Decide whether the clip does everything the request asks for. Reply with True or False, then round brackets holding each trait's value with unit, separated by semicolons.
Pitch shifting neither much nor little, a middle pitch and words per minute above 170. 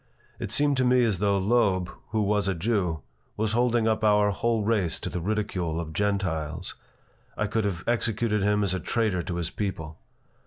False (3.6 semitones; 105 Hz; 190 wpm)